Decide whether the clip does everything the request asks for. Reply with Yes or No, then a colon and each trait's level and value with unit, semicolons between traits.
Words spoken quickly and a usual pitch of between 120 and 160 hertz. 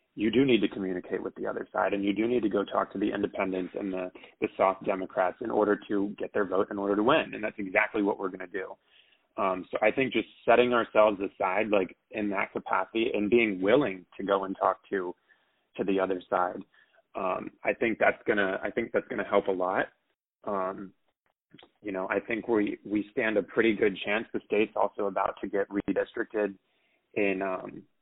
No: fast, 210 wpm; low, 100 Hz